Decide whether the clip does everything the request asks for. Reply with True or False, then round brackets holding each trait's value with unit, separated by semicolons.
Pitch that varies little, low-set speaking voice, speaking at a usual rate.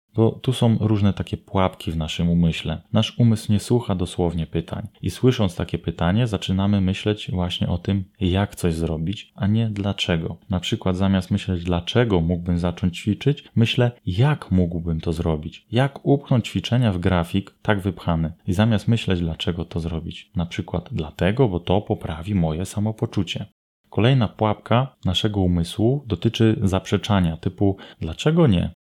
False (3.9 semitones; 100 Hz; 150 wpm)